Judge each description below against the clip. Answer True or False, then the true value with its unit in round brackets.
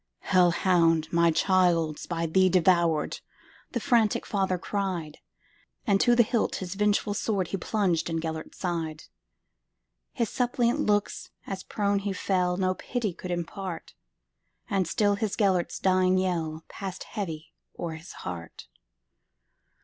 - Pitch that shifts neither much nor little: True (3.4 semitones)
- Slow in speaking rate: True (120 wpm)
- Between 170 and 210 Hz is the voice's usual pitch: True (185 Hz)